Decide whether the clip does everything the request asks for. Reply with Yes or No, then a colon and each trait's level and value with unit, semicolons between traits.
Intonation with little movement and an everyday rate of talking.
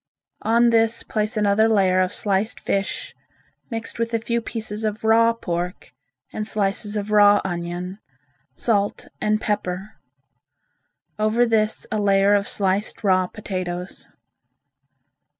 No: narrow, 2.2 semitones; slow, 125 wpm